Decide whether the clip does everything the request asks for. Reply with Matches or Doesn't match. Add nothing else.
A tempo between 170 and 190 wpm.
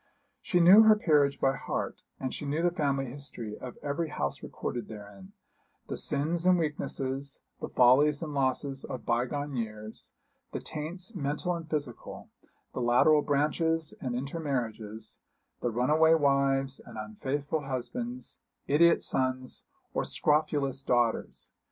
Doesn't match